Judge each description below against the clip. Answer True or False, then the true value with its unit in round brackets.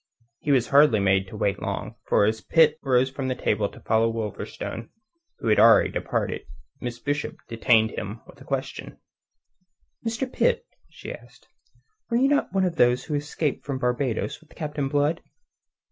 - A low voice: True (130 Hz)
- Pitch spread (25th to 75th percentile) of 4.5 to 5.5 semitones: True (4.9 semitones)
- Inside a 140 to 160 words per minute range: False (170 wpm)